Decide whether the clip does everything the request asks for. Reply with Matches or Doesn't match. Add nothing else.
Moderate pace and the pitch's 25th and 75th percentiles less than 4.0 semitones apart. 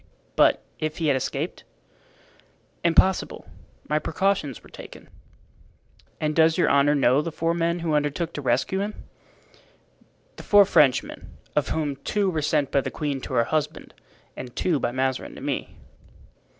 Matches